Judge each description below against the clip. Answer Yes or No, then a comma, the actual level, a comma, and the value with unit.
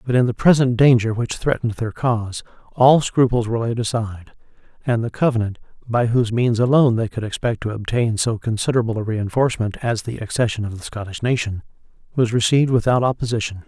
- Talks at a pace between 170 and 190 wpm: Yes, average, 180 wpm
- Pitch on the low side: Yes, low, 115 Hz